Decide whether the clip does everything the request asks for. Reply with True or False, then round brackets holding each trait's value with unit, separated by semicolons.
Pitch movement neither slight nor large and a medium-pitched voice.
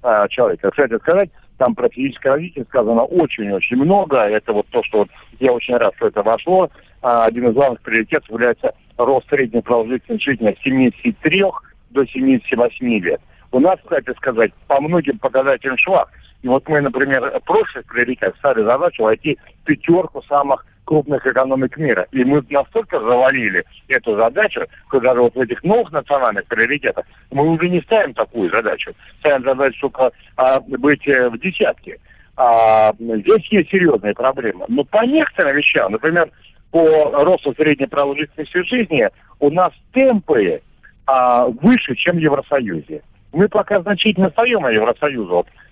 False (8.7 semitones; 145 Hz)